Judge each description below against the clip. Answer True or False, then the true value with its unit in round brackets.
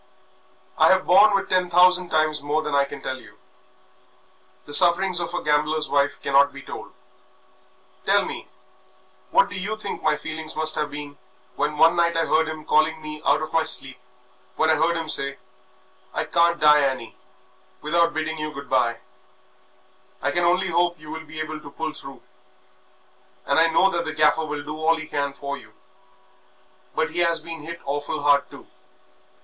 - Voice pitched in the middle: True (155 Hz)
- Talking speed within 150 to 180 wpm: False (190 wpm)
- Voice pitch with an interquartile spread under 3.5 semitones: True (2.5 semitones)